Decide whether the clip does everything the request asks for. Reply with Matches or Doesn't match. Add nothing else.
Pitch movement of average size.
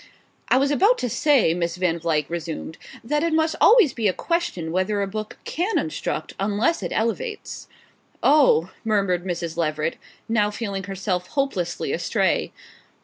Doesn't match